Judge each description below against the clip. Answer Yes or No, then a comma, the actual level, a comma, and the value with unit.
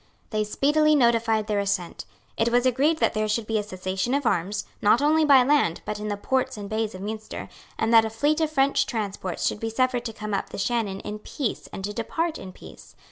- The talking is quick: Yes, fast, 230 wpm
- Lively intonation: No, average, 4.0 semitones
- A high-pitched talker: Yes, high, 225 Hz